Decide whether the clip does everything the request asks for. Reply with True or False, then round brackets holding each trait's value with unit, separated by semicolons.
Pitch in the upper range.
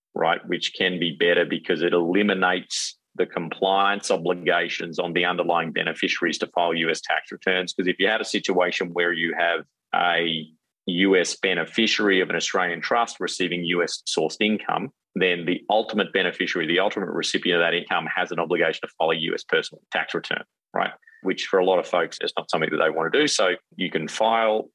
False (90 Hz)